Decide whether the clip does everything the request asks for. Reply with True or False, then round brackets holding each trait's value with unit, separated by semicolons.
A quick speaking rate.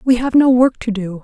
True (290 wpm)